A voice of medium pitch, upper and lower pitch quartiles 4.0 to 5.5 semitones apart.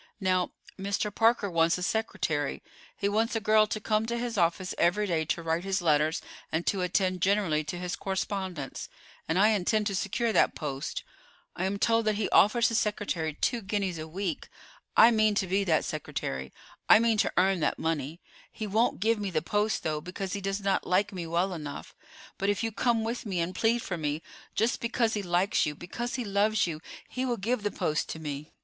No: high, 195 Hz; average, 4.3 semitones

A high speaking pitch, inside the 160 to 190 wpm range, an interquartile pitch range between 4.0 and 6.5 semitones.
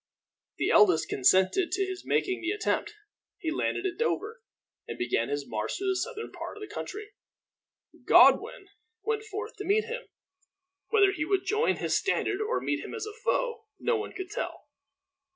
No: very high, 400 Hz; average, 175 wpm; average, 3.4 semitones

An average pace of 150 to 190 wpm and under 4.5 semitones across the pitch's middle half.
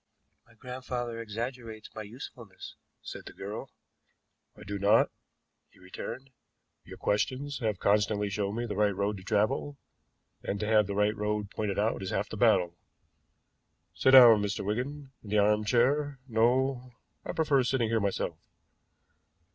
Yes: average, 155 wpm; average, 3.5 semitones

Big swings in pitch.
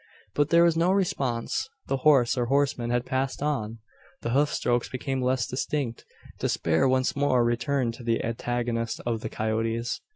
No: average, 3.2 semitones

